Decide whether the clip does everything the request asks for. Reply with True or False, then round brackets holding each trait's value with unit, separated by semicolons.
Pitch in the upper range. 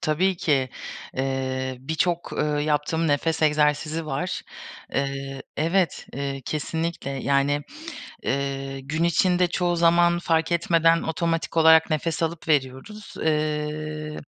False (155 Hz)